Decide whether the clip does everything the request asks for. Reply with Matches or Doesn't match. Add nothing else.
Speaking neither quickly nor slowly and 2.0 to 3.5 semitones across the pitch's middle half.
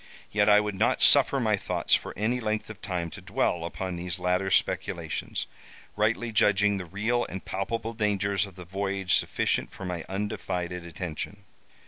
Matches